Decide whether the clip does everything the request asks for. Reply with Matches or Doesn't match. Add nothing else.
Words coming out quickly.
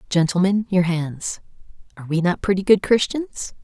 Doesn't match